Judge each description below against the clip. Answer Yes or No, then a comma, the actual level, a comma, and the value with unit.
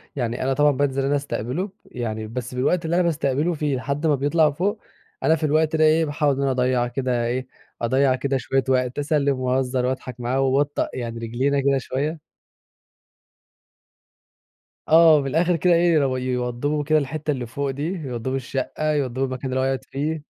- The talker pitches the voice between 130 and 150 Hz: Yes, low, 135 Hz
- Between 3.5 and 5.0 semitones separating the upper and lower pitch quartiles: No, average, 3.0 semitones